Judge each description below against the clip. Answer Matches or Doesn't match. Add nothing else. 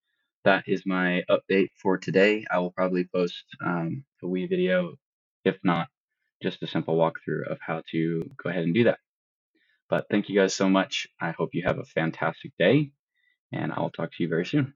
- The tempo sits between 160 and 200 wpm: Matches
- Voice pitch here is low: Matches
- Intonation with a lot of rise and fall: Matches